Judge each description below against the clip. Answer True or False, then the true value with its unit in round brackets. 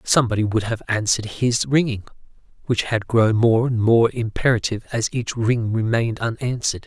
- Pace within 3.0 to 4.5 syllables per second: False (5.4 syllables/s)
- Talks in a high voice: False (115 Hz)